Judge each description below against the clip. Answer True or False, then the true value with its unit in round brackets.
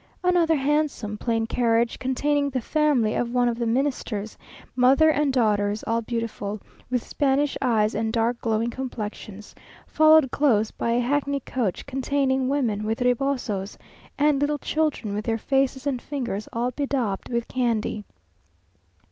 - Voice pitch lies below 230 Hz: False (245 Hz)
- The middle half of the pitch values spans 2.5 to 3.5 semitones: False (3.9 semitones)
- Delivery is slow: False (145 wpm)